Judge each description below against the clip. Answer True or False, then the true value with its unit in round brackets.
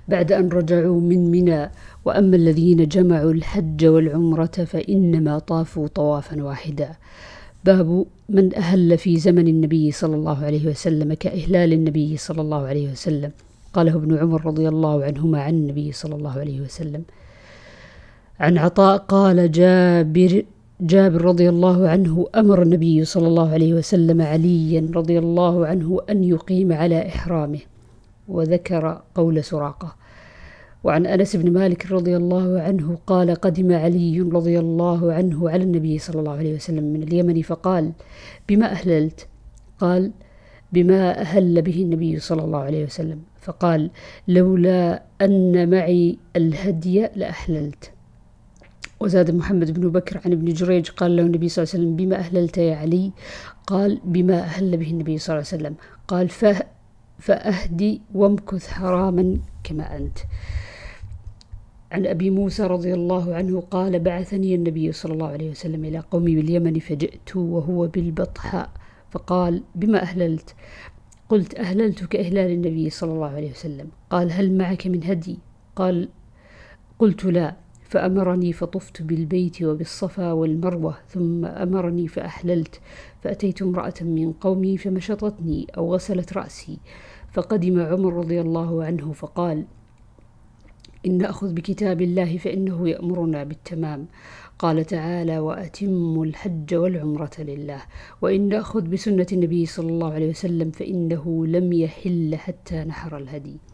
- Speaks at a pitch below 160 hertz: False (170 Hz)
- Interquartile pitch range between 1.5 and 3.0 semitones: True (2.4 semitones)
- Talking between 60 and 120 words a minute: False (130 wpm)